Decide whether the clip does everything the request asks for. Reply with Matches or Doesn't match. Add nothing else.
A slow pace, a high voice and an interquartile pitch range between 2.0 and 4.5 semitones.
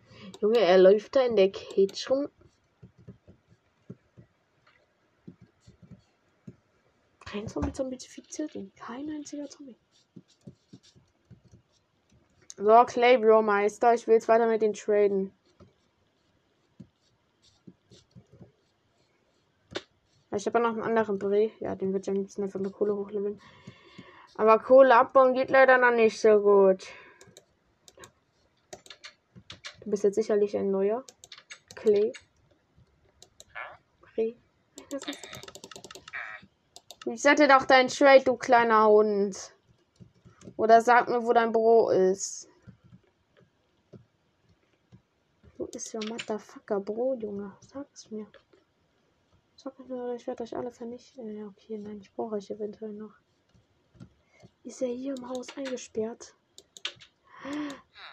Matches